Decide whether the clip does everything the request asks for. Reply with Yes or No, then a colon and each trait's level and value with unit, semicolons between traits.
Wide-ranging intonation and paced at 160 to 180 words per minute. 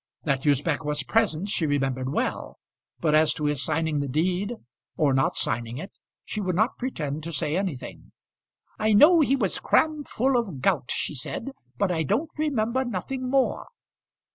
Yes: wide, 7.9 semitones; average, 170 wpm